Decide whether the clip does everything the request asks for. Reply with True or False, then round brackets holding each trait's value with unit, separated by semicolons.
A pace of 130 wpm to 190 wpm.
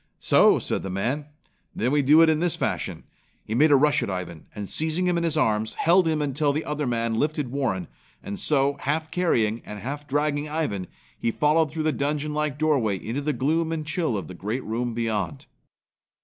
False (205 wpm)